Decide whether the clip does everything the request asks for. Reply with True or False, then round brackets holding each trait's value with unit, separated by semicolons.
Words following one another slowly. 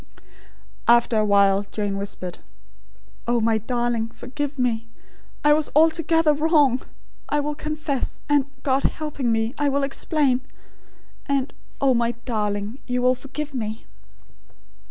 True (130 wpm)